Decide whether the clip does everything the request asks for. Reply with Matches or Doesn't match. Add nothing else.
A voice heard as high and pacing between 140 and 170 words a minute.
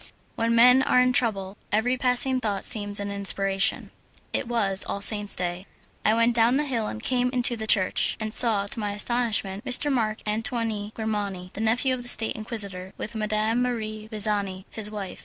Doesn't match